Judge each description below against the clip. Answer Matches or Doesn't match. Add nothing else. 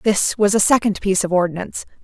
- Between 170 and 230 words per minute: Matches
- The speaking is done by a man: Doesn't match